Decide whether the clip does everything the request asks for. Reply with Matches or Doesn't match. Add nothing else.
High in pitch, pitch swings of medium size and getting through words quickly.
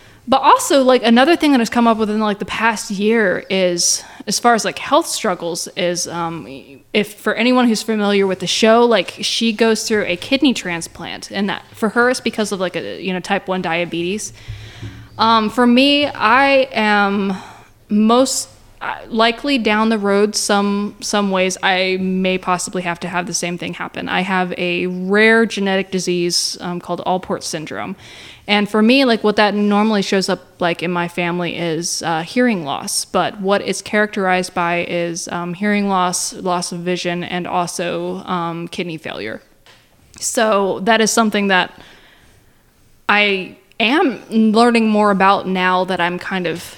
Doesn't match